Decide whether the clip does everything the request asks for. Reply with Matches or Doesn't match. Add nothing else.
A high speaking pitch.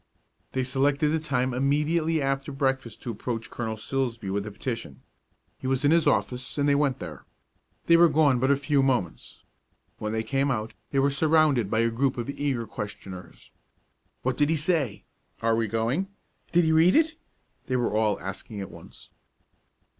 Doesn't match